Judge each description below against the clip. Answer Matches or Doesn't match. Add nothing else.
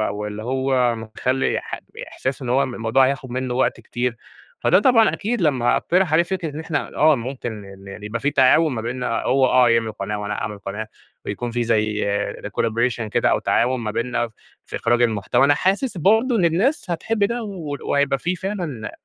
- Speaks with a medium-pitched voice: Doesn't match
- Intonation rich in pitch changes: Matches